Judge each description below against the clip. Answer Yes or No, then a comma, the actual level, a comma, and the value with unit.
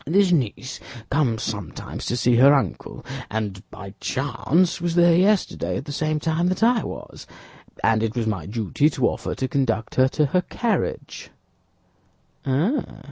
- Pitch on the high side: No, low, 135 Hz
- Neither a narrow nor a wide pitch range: No, wide, 7.2 semitones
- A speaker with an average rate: Yes, average, 155 wpm